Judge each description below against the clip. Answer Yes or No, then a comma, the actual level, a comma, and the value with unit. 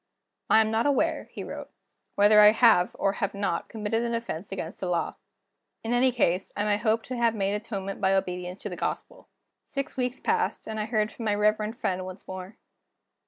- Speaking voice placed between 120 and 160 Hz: No, high, 210 Hz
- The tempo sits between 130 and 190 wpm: No, fast, 205 wpm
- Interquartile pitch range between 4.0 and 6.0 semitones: No, average, 3.0 semitones